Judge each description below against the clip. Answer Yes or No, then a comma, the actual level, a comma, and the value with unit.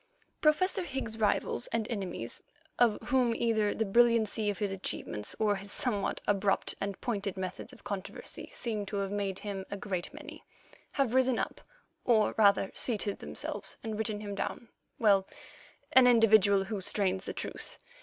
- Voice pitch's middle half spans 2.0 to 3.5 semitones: Yes, average, 2.7 semitones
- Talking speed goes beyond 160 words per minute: No, average, 155 wpm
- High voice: Yes, high, 210 Hz